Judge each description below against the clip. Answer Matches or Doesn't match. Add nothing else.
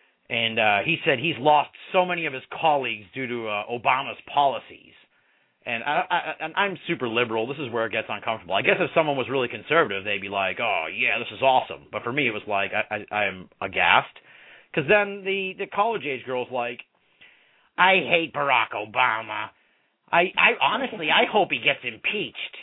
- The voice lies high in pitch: Doesn't match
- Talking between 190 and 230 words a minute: Matches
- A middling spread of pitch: Doesn't match